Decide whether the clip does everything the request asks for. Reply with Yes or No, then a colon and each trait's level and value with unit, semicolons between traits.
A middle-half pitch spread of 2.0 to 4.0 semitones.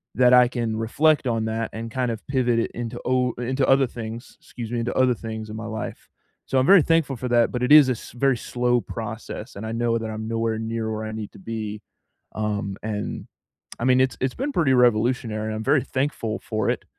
Yes: narrow, 2.5 semitones